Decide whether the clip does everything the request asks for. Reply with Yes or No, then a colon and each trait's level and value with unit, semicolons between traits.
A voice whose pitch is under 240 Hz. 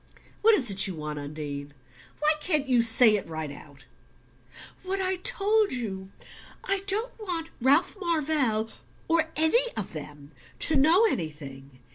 No: very high, 255 Hz